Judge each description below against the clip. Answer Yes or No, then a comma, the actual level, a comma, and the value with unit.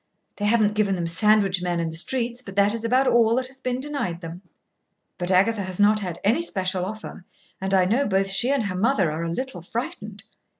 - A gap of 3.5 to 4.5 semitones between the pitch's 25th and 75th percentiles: Yes, average, 4.1 semitones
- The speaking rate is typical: No, fast, 220 wpm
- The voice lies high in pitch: Yes, high, 205 Hz